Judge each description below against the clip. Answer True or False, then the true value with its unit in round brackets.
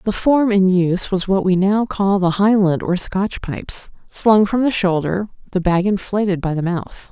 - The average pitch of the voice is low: False (195 Hz)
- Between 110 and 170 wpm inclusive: False (195 wpm)